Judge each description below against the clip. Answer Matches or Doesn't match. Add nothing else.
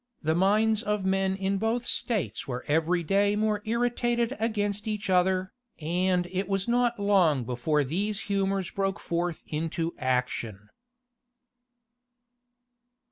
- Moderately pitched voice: Doesn't match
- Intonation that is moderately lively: Matches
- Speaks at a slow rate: Matches